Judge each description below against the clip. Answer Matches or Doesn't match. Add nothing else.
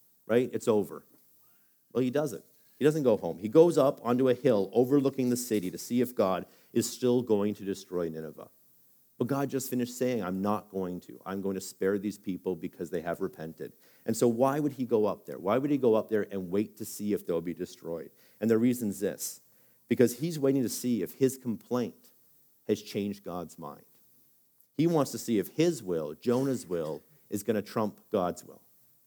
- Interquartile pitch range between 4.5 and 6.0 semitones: Matches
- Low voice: Matches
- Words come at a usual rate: Doesn't match